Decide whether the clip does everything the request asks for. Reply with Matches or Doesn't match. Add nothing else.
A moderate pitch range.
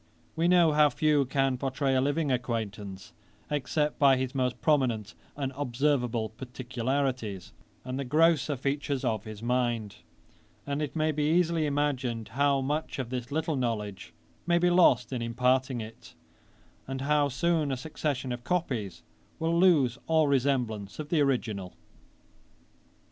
Matches